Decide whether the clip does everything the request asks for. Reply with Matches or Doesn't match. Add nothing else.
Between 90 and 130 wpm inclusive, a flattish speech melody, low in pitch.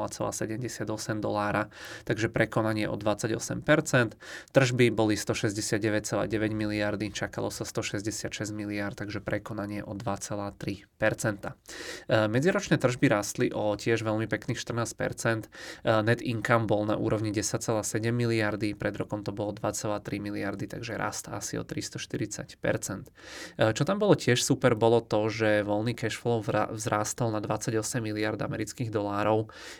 Matches